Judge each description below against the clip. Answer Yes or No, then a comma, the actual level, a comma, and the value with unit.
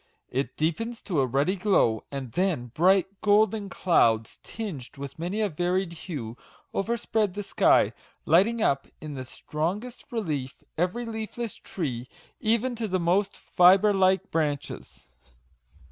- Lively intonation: Yes, wide, 6.2 semitones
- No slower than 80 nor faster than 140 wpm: Yes, slow, 135 wpm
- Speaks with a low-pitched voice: No, medium, 185 Hz